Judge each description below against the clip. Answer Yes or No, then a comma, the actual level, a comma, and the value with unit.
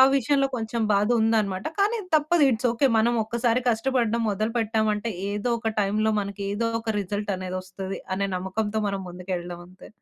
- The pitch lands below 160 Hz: No, high, 220 Hz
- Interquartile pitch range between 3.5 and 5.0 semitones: No, average, 3.0 semitones